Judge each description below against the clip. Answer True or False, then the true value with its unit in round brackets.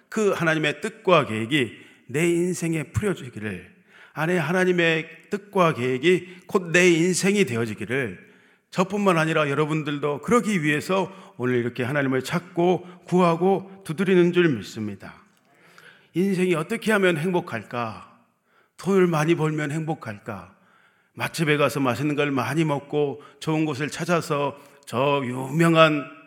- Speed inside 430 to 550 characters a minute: False (290 characters per minute)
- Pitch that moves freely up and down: False (4.3 semitones)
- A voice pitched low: False (160 Hz)